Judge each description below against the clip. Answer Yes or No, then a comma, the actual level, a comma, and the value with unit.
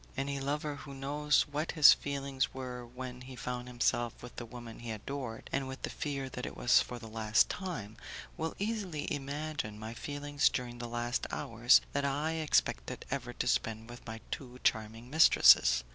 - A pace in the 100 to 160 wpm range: No, average, 180 wpm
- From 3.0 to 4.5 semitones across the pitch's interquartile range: Yes, average, 3.3 semitones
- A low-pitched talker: Yes, low, 125 Hz